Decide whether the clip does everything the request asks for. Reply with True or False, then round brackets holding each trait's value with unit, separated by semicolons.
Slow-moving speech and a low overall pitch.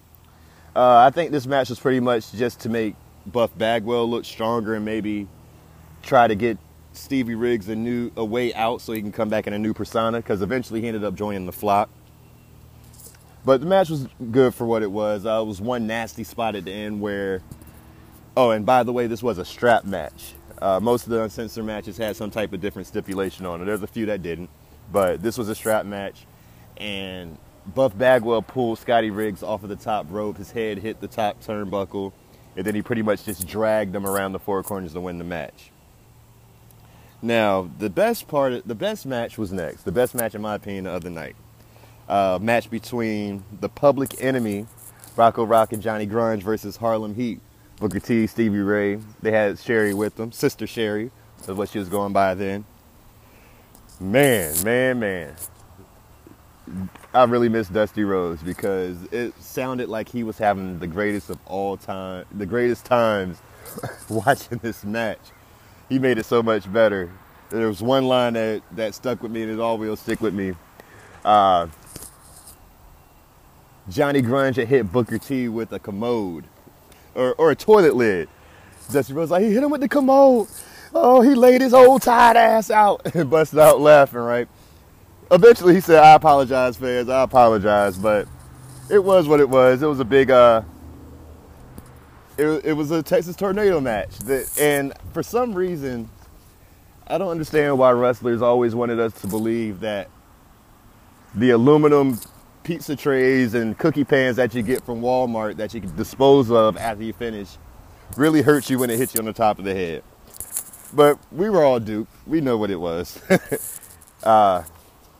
False (185 wpm; 110 Hz)